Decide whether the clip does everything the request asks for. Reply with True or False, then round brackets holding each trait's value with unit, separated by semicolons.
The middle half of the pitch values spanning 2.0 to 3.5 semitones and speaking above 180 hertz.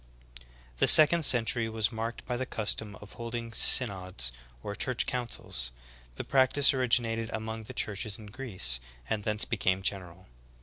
False (3.1 semitones; 110 Hz)